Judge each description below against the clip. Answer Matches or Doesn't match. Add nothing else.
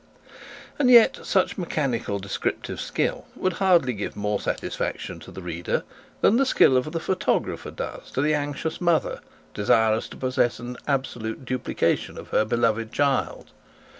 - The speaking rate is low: Doesn't match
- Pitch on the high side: Doesn't match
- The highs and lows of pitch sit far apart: Matches